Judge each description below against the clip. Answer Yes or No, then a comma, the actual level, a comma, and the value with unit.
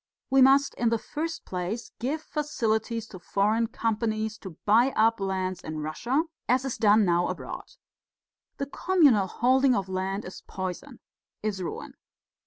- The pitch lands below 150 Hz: No, high, 220 Hz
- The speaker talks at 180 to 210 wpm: No, average, 150 wpm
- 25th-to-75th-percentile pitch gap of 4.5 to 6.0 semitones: Yes, average, 5.3 semitones